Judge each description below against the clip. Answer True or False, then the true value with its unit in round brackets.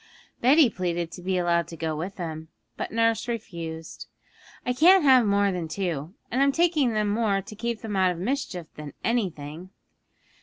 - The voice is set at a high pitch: True (195 Hz)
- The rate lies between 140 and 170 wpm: False (180 wpm)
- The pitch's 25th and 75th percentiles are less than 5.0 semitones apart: False (5.6 semitones)